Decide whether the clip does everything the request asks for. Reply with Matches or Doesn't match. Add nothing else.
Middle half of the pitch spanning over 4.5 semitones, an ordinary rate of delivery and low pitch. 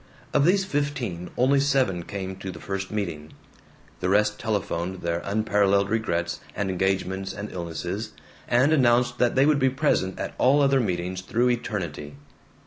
Matches